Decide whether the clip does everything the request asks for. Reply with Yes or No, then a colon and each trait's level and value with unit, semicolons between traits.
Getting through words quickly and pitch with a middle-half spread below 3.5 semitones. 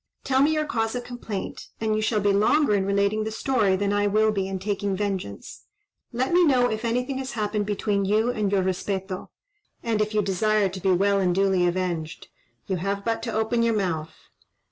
Yes: fast, 210 wpm; average, 2.8 semitones